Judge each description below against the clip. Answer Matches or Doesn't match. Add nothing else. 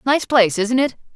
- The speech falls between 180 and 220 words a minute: Matches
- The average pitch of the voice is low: Doesn't match